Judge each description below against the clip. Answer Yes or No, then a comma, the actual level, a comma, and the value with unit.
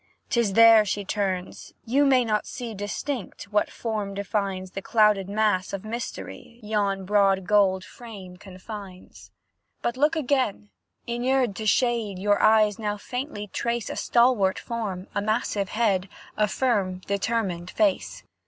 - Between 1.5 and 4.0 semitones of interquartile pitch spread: Yes, average, 3.2 semitones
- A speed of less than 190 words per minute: Yes, average, 140 wpm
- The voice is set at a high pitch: Yes, high, 210 Hz